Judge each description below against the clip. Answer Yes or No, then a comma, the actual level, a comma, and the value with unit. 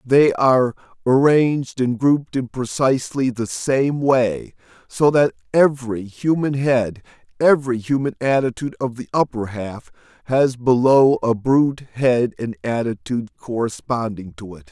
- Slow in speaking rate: Yes, slow, 130 wpm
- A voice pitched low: Yes, low, 125 Hz